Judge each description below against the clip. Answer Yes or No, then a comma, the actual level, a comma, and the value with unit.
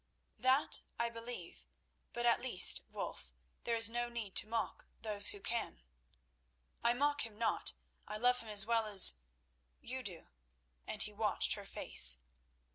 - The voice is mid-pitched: No, high, 225 Hz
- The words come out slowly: No, average, 150 wpm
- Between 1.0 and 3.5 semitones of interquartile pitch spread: No, average, 4.4 semitones